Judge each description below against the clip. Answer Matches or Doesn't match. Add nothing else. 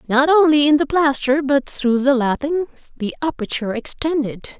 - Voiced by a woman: Matches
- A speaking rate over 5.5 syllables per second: Doesn't match